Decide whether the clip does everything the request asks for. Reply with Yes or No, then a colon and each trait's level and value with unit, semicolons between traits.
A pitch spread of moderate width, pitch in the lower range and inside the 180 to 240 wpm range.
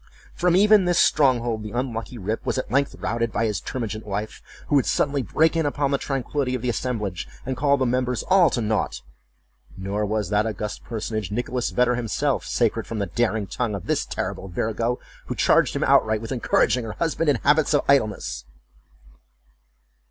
Yes: average, 4.3 semitones; low, 120 Hz; average, 185 wpm